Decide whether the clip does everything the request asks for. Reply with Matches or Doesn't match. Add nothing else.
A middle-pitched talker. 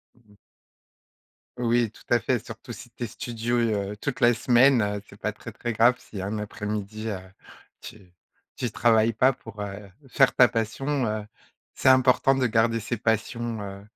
Doesn't match